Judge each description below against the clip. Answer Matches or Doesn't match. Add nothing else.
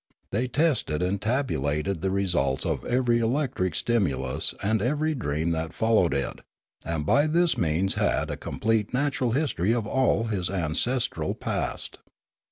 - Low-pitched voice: Matches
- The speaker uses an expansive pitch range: Matches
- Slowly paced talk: Doesn't match